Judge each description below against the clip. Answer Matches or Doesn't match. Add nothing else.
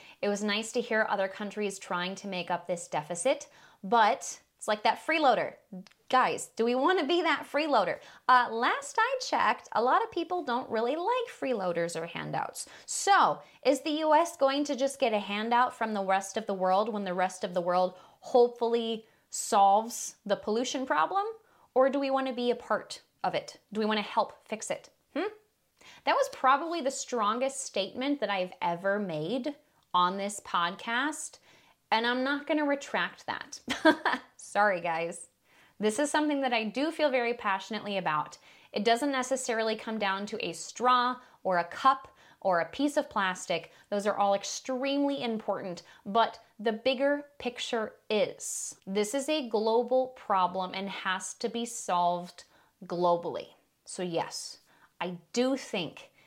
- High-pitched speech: Matches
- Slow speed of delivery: Doesn't match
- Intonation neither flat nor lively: Doesn't match